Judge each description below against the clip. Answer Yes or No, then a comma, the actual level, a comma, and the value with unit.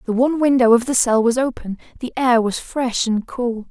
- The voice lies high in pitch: Yes, high, 245 Hz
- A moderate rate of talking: No, fast, 225 wpm